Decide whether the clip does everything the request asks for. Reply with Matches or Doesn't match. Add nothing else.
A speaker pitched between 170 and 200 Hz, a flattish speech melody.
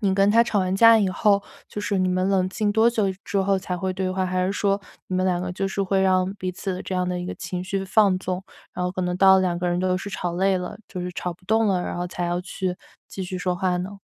Matches